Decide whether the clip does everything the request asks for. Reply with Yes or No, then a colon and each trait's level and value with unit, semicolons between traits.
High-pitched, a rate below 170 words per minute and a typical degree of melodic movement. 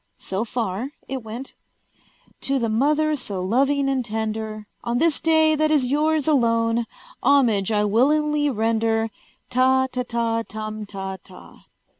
Yes: high, 235 Hz; average, 140 wpm; average, 4.4 semitones